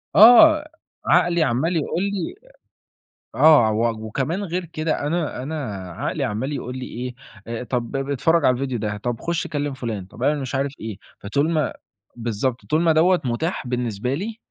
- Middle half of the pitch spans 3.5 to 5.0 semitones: No, wide, 5.4 semitones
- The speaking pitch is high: No, medium, 140 Hz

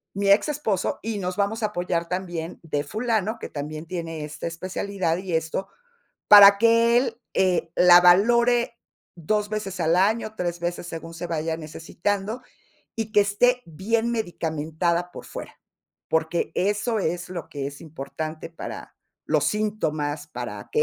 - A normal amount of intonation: Yes, average, 4.6 semitones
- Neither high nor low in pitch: Yes, medium, 180 Hz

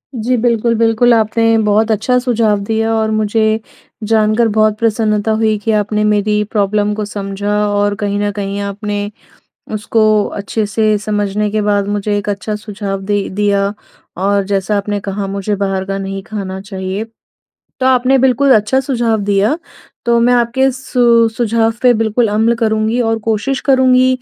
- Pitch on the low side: No, high, 215 Hz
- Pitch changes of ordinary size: No, narrow, 2.0 semitones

